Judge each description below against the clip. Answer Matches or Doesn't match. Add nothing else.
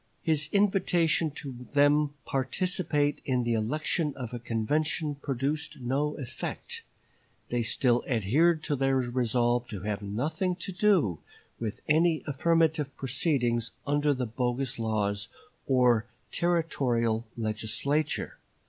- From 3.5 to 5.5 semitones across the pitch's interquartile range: Matches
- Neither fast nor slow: Doesn't match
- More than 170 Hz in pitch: Doesn't match